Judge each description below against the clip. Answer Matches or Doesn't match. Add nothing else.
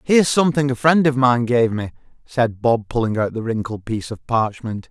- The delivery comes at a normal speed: Doesn't match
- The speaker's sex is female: Doesn't match